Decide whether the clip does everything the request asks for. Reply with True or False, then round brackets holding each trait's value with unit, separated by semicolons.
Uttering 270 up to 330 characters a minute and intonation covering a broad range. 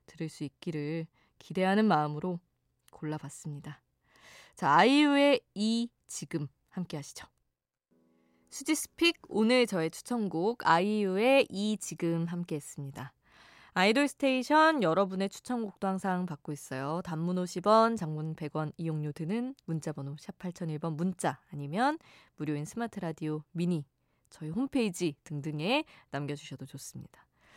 True (285 characters per minute; 6.1 semitones)